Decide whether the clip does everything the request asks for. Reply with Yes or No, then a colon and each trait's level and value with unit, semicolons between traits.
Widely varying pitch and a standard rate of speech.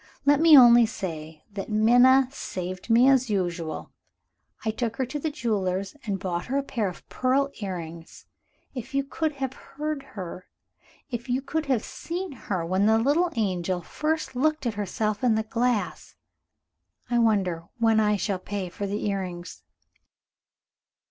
Yes: wide, 5.8 semitones; average, 160 wpm